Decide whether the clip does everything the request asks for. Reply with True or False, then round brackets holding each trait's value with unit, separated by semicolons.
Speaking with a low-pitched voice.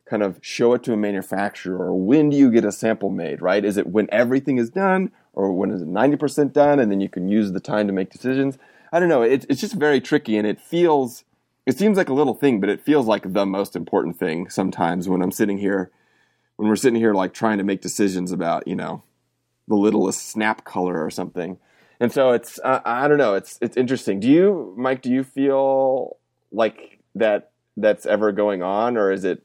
True (110 Hz)